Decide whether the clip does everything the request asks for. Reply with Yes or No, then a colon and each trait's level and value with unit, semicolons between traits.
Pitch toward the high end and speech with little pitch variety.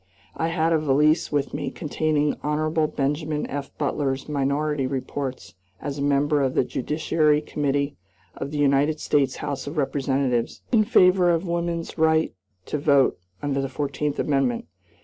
No: medium, 145 Hz; narrow, 2.1 semitones